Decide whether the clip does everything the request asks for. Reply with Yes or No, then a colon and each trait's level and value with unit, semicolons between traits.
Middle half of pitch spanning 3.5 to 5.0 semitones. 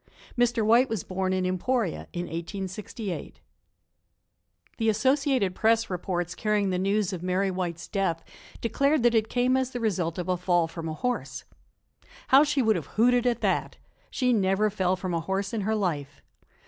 Yes: average, 4.5 semitones